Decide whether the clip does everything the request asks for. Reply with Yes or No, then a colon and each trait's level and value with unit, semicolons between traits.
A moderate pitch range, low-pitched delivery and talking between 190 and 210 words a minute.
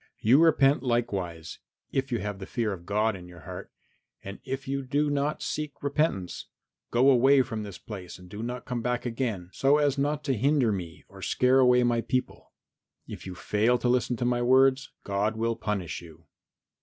Yes: average, 4.7 semitones; low, 120 Hz; average, 195 wpm